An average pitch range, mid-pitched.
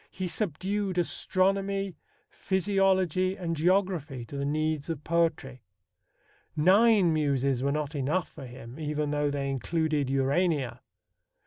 Yes: average, 4.9 semitones; medium, 160 Hz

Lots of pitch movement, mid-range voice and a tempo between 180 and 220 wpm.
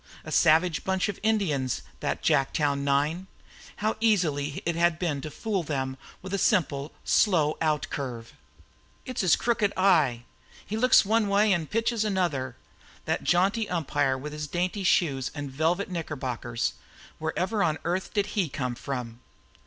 No: wide, 5.8 semitones; medium, 165 Hz; average, 150 wpm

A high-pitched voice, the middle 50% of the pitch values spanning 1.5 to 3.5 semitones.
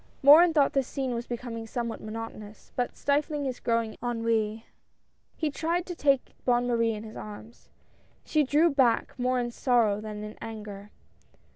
No: high, 240 Hz; average, 3.9 semitones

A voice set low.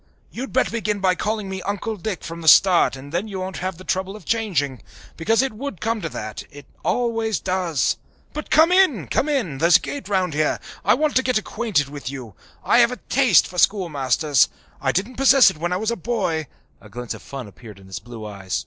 No: medium, 185 Hz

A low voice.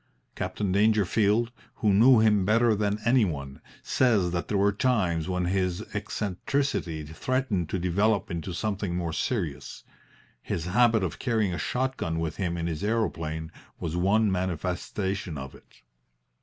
Yes: very low, 95 Hz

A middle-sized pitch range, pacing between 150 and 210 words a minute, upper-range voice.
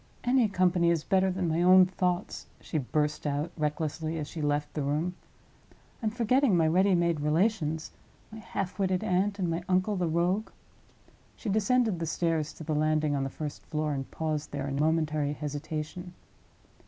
No: average, 3.5 semitones; average, 170 wpm; medium, 165 Hz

